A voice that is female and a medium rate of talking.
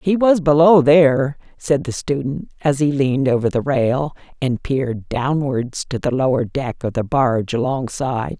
Yes: female; average, 170 wpm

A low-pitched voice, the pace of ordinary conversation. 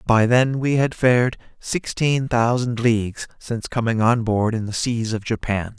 Yes: low, 115 Hz; average, 175 wpm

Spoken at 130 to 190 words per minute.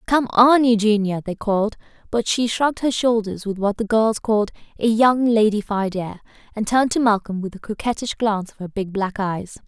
No: average, 200 wpm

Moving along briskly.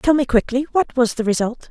Yes: fast, 210 wpm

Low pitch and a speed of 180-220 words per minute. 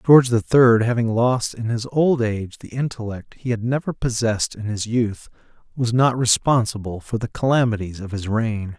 Yes: low, 115 Hz; average, 185 wpm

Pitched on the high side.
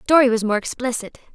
Yes: high, 240 Hz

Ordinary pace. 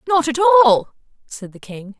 Yes: average, 180 wpm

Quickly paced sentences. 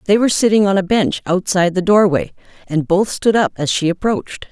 Yes: fast, 215 wpm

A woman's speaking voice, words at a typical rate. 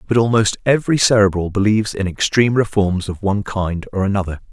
No: male; average, 175 wpm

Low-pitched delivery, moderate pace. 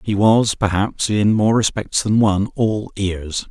Yes: low, 105 Hz; average, 170 wpm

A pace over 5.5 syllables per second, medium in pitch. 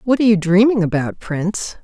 No: 5.9 syllables/s; high, 200 Hz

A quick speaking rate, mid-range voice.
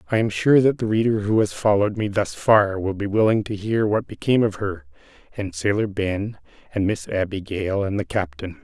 No: fast, 210 wpm; low, 105 Hz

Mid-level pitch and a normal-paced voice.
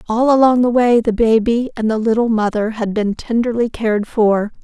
No: high, 225 Hz; average, 195 wpm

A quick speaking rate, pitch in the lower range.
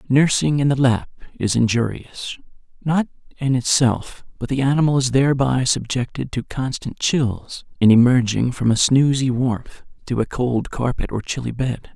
No: average, 155 wpm; low, 130 Hz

